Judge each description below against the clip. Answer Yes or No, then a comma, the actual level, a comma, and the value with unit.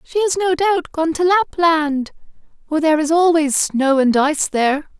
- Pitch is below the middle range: No, very high, 315 Hz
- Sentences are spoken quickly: No, average, 180 wpm